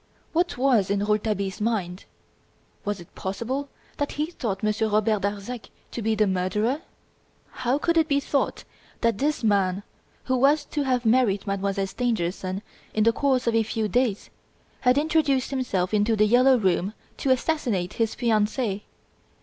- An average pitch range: Yes, average, 4.4 semitones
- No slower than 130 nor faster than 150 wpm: No, average, 160 wpm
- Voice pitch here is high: Yes, high, 225 Hz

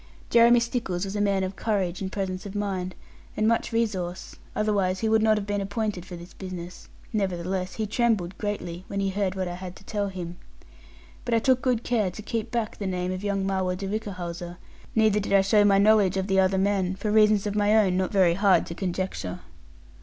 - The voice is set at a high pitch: Yes, high, 195 Hz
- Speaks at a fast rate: Yes, fast, 215 wpm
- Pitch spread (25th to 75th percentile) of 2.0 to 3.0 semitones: Yes, narrow, 2.5 semitones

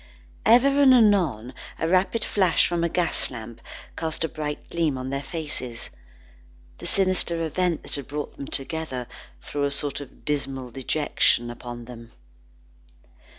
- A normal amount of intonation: Yes, average, 5.0 semitones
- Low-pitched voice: No, medium, 150 Hz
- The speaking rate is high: No, average, 150 wpm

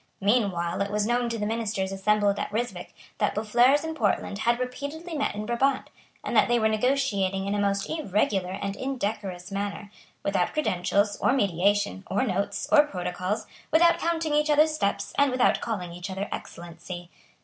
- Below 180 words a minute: Yes, average, 170 wpm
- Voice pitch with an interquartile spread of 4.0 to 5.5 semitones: Yes, average, 4.5 semitones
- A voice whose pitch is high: Yes, high, 210 Hz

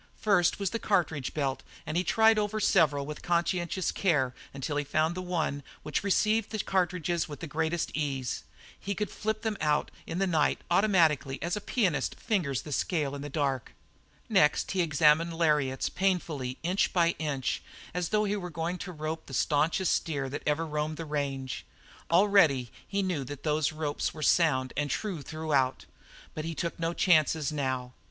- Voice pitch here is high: No, medium, 160 Hz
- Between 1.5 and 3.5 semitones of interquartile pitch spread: No, average, 3.9 semitones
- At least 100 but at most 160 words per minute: No, average, 185 wpm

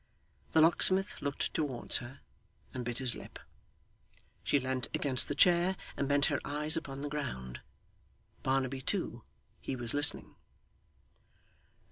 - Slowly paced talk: Yes, slow, 130 wpm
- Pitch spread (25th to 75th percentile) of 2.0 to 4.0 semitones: Yes, average, 2.7 semitones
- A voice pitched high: No, medium, 140 Hz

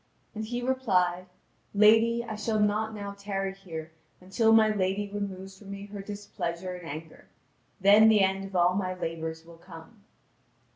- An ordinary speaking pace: Yes, average, 160 wpm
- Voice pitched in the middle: No, high, 195 Hz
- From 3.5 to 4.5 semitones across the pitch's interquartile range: No, average, 2.8 semitones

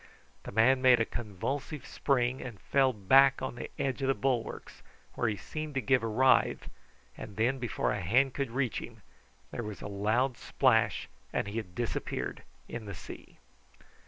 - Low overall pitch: Yes, low, 120 Hz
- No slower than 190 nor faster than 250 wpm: No, average, 180 wpm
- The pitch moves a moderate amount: Yes, average, 3.5 semitones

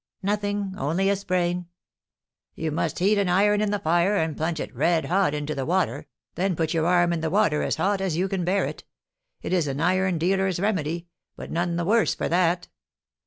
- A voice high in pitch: No, medium, 180 Hz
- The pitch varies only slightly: No, average, 3.0 semitones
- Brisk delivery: Yes, fast, 210 wpm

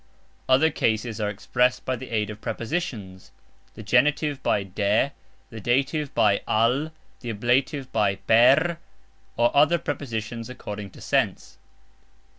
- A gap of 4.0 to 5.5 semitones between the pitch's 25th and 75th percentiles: Yes, average, 4.6 semitones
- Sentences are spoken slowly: Yes, slow, 130 wpm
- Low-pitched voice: Yes, low, 120 Hz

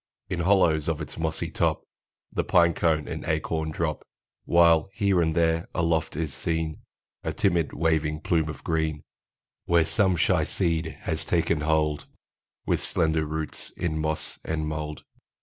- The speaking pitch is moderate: No, very low, 80 Hz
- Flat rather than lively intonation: Yes, narrow, 1.4 semitones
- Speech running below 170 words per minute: Yes, average, 155 wpm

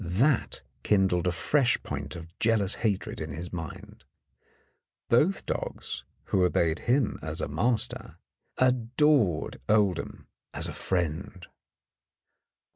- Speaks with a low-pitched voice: Yes, very low, 95 Hz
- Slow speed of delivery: Yes, slow, 115 wpm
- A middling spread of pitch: No, wide, 6.0 semitones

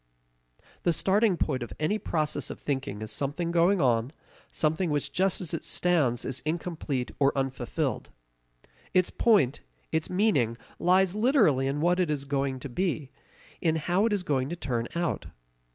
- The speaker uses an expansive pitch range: No, average, 4.8 semitones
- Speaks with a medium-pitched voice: Yes, medium, 155 Hz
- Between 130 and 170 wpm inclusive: Yes, average, 165 wpm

